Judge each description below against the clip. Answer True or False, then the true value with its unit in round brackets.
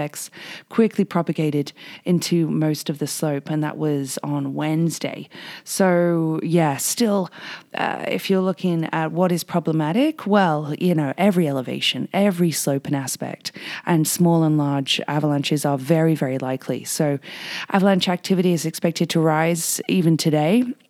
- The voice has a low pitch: False (160 Hz)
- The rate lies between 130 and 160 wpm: True (145 wpm)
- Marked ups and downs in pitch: False (3.0 semitones)